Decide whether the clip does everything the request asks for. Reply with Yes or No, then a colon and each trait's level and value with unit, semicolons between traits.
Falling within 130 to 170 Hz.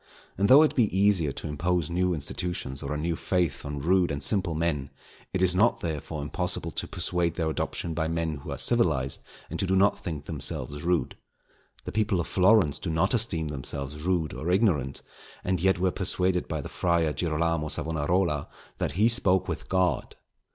No: very low, 85 Hz